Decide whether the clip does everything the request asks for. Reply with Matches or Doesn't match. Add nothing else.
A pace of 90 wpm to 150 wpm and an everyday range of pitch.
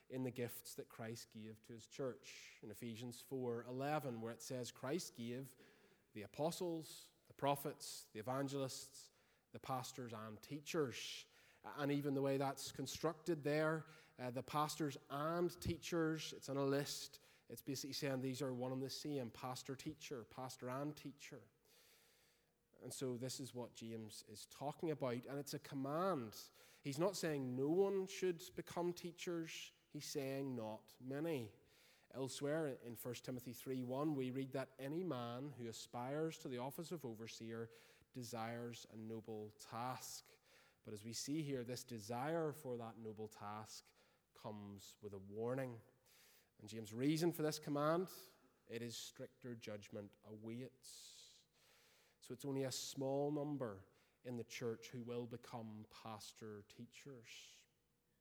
Matches